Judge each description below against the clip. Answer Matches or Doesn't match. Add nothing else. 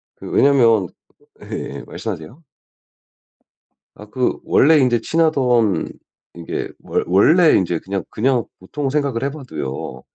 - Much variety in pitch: Matches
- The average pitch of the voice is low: Matches